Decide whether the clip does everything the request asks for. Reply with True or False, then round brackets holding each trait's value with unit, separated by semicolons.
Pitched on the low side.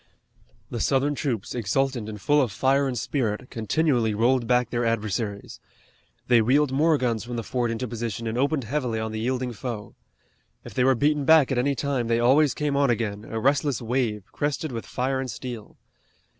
True (125 Hz)